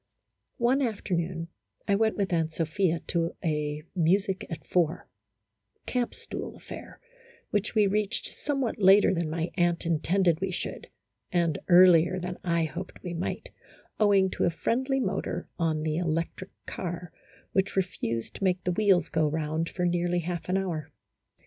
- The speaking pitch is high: No, medium, 175 Hz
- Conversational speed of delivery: Yes, average, 155 wpm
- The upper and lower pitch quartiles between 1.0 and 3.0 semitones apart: Yes, average, 2.7 semitones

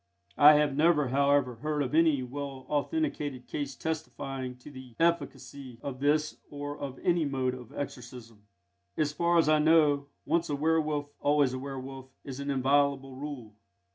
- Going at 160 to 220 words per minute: Yes, average, 165 wpm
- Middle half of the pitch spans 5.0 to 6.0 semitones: No, narrow, 2.4 semitones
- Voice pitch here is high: No, medium, 140 Hz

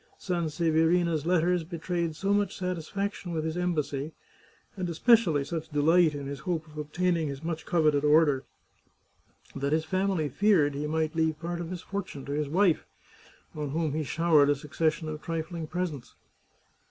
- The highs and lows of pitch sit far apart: No, narrow, 2.6 semitones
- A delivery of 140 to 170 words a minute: Yes, average, 165 wpm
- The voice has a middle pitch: Yes, medium, 160 Hz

